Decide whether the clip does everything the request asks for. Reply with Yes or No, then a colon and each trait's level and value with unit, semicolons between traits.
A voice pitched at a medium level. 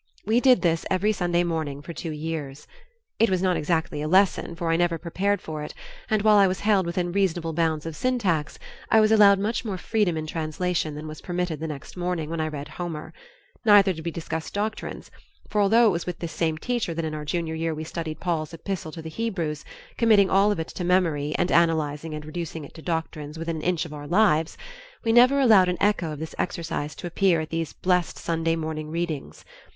Yes: medium, 170 Hz